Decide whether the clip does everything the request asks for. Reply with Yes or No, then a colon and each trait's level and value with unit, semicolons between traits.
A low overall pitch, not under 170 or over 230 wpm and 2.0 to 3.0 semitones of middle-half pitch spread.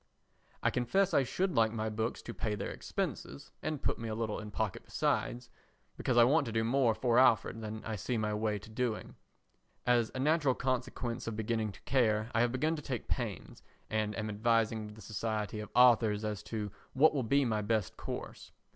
Yes: low, 115 Hz; average, 200 wpm; average, 2.7 semitones